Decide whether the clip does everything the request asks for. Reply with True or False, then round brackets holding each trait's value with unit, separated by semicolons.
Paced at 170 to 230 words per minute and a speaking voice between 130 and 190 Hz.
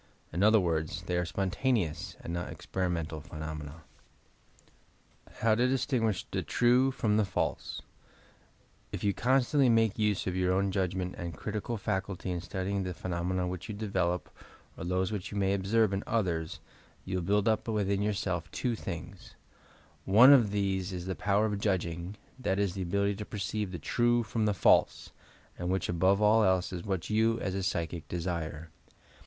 False (175 wpm; 95 Hz)